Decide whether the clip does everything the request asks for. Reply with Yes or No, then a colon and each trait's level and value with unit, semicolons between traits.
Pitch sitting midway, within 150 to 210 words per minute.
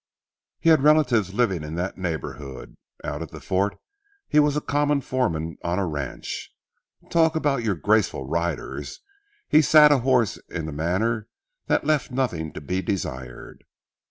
No: low, 100 Hz; average, 155 wpm